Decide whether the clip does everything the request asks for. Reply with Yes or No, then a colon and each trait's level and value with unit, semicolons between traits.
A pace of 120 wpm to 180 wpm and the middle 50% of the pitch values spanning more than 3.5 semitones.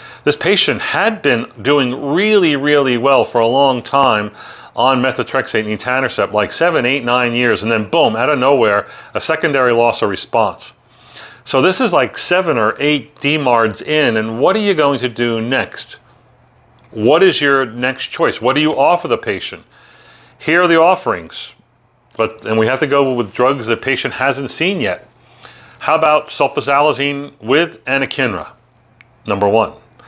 No: average, 170 wpm; average, 3.2 semitones